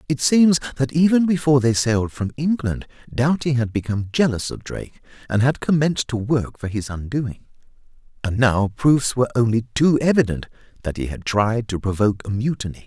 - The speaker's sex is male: Yes, male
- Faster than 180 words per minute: Yes, average, 190 wpm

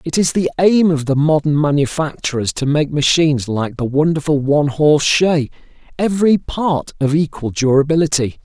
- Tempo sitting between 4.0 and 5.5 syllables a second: Yes, 5.2 syllables/s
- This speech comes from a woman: No, male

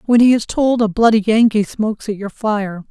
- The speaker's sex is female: Yes, female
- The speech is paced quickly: Yes, fast, 225 wpm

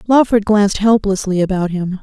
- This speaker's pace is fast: No, average, 150 wpm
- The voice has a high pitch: Yes, high, 200 Hz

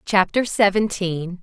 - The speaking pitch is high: Yes, high, 195 Hz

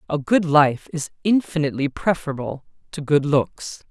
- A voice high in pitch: No, medium, 155 Hz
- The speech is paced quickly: No, average, 140 wpm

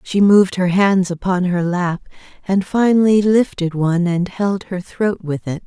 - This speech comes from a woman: Yes, female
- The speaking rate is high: No, average, 180 wpm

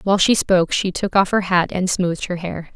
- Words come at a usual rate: No, fast, 260 wpm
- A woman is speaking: Yes, female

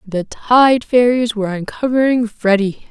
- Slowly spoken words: Yes, slow, 125 wpm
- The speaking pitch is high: Yes, high, 225 Hz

